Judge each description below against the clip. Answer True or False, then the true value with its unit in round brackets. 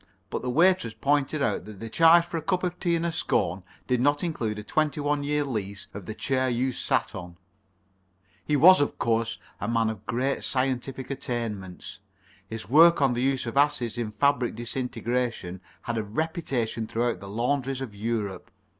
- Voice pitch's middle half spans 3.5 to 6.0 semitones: True (4.5 semitones)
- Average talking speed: True (185 wpm)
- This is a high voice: False (125 Hz)